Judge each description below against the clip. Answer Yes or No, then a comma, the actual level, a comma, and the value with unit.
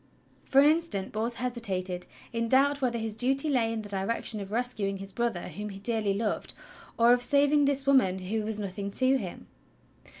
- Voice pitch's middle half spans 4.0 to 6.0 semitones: Yes, average, 4.6 semitones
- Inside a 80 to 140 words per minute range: No, average, 195 wpm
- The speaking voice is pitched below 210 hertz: No, high, 230 Hz